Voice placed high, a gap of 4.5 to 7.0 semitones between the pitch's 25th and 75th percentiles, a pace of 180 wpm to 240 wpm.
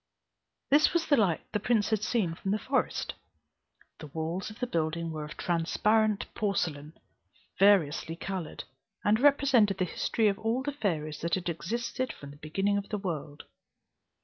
No: high, 195 Hz; average, 5.2 semitones; average, 165 wpm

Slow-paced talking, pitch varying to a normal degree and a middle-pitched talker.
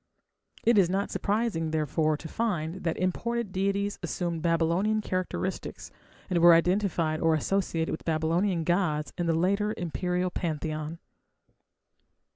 Yes: slow, 125 wpm; average, 3.4 semitones; medium, 175 Hz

